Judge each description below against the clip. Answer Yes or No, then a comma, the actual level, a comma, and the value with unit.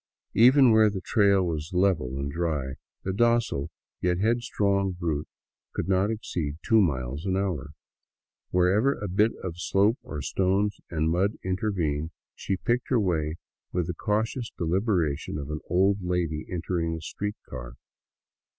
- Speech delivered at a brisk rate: No, average, 150 wpm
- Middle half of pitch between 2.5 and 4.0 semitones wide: No, average, 4.4 semitones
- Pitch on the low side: Yes, very low, 90 Hz